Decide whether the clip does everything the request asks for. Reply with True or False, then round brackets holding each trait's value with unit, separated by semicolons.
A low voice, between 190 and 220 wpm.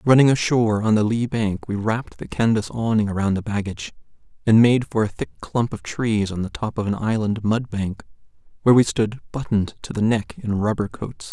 True (110 Hz; 205 wpm)